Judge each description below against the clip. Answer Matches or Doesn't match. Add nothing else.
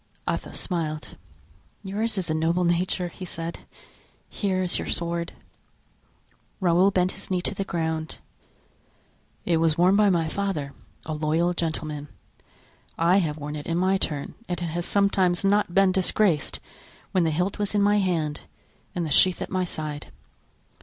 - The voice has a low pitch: Doesn't match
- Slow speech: Doesn't match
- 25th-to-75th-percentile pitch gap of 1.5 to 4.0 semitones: Matches